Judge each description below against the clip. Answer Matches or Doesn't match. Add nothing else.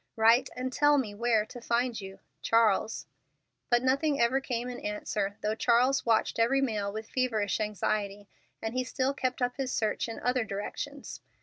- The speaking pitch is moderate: Doesn't match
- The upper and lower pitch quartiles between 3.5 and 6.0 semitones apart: Doesn't match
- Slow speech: Doesn't match